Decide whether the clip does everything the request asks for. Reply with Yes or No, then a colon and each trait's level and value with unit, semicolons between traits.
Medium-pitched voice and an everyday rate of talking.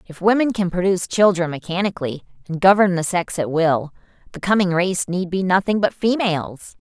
Yes: medium, 180 Hz; average, 175 wpm